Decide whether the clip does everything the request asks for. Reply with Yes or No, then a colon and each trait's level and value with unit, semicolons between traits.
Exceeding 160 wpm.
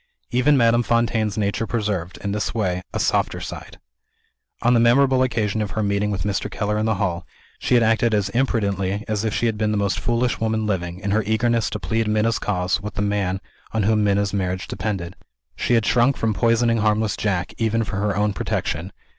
Yes: fast, 205 wpm